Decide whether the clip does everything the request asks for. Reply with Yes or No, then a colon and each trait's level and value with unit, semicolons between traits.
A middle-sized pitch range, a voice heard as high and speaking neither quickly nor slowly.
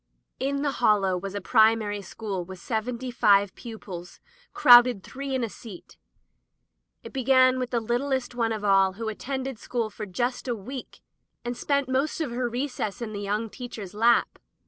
Yes: average, 3.8 semitones; high, 235 Hz; average, 175 wpm